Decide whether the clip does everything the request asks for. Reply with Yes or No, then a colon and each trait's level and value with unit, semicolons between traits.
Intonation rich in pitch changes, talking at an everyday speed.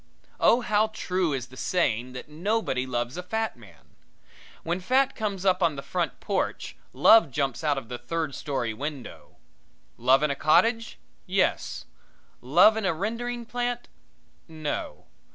Yes: wide, 8.4 semitones; average, 150 wpm